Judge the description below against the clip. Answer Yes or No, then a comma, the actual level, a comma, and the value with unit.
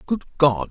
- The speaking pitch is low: Yes, low, 130 Hz